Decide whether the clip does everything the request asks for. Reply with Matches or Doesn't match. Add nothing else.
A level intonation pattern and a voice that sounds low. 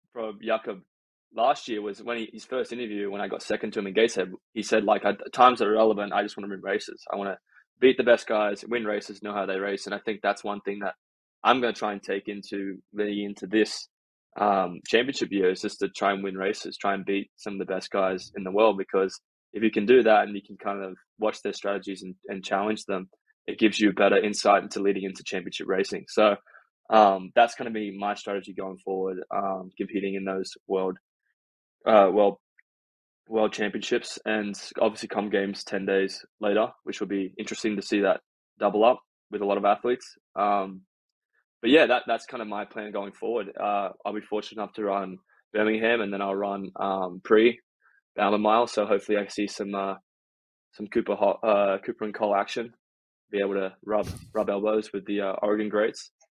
Matches